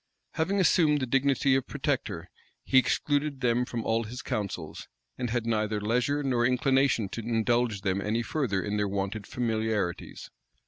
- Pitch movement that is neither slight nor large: Yes, average, 3.9 semitones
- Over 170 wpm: No, average, 155 wpm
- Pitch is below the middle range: Yes, low, 120 Hz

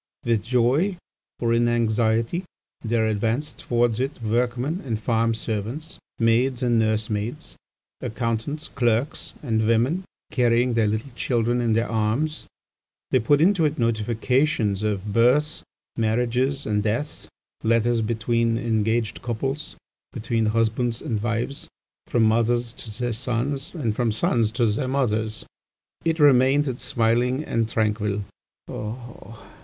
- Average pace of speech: No, slow, 125 wpm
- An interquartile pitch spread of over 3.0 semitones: No, narrow, 2.5 semitones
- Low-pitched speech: Yes, low, 115 Hz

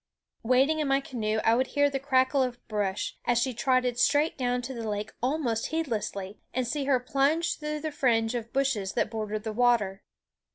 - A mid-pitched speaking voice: No, very high, 250 Hz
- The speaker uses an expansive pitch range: No, average, 3.6 semitones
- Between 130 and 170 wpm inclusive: No, average, 195 wpm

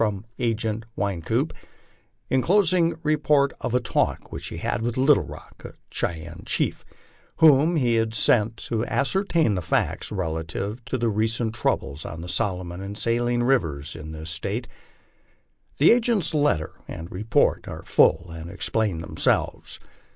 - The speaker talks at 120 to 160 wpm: Yes, average, 150 wpm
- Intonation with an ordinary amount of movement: No, wide, 7.3 semitones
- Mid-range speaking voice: No, low, 110 Hz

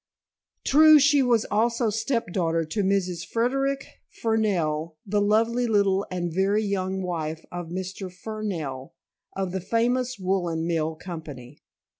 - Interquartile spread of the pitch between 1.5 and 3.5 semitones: No, average, 4.9 semitones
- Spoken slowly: Yes, slow, 130 wpm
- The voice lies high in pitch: Yes, high, 195 Hz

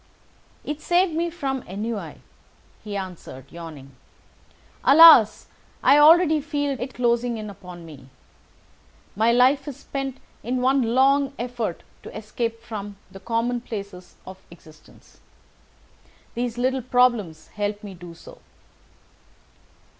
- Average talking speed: No, slow, 120 wpm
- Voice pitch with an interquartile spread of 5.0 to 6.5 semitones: Yes, average, 5.3 semitones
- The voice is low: No, high, 235 Hz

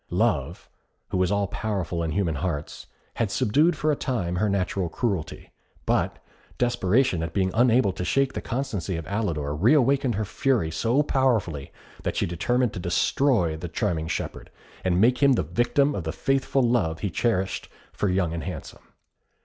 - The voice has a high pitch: No, low, 100 Hz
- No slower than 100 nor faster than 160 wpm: No, average, 175 wpm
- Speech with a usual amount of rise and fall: No, wide, 6.4 semitones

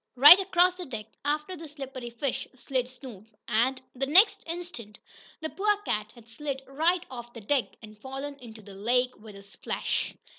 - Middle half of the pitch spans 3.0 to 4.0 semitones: No, average, 4.8 semitones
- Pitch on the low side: No, very high, 260 Hz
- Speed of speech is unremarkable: Yes, average, 180 wpm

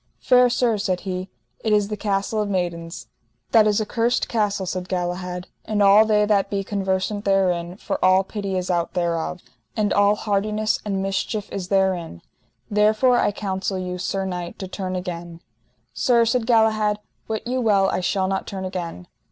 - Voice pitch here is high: Yes, high, 195 Hz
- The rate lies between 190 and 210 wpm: No, average, 175 wpm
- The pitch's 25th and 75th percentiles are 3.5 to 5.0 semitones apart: No, narrow, 2.6 semitones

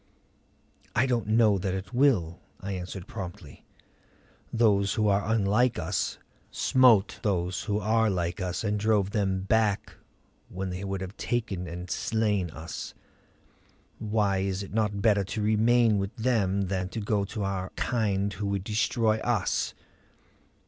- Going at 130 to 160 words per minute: Yes, average, 150 wpm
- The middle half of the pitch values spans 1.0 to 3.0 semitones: Yes, average, 2.7 semitones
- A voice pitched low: Yes, low, 100 Hz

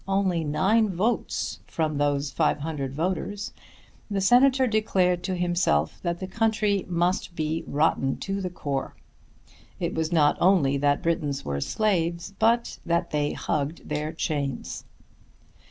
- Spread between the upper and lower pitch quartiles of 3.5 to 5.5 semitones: Yes, average, 4.8 semitones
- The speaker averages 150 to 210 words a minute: No, slow, 135 wpm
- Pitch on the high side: No, medium, 170 Hz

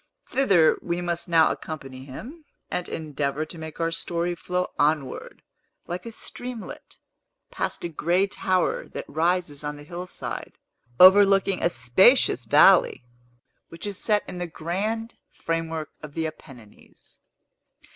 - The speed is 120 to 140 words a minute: Yes, slow, 135 wpm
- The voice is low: No, medium, 170 Hz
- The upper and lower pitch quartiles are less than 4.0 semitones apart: Yes, average, 3.5 semitones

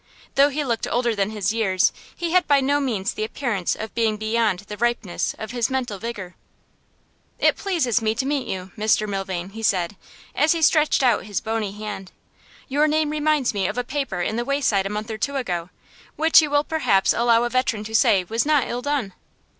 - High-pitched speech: Yes, high, 230 Hz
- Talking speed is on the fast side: Yes, fast, 210 wpm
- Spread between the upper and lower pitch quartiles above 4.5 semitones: Yes, average, 5.2 semitones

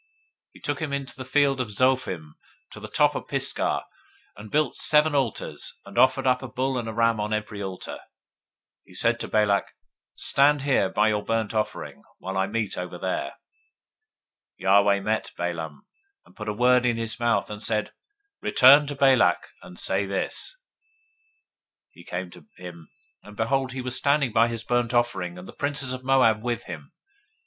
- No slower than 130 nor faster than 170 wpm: No, average, 190 wpm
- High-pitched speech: No, low, 115 Hz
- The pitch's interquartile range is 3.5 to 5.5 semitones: Yes, average, 4.6 semitones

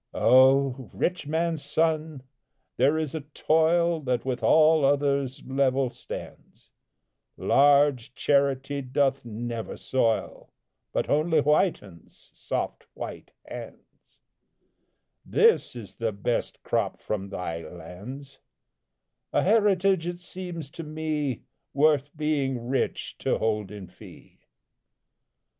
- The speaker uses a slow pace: Yes, slow, 110 wpm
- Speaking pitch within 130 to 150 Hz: Yes, medium, 140 Hz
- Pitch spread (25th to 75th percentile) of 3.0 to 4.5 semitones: Yes, average, 3.9 semitones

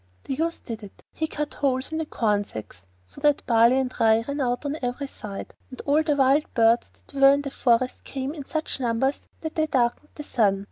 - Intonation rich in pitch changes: No, average, 3.9 semitones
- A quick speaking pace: Yes, fast, 225 wpm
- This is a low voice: No, very high, 265 Hz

